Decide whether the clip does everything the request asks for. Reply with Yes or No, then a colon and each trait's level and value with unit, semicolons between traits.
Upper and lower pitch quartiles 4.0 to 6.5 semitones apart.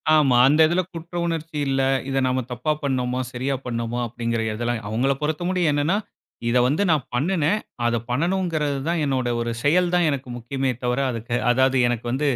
Yes: average, 4.4 semitones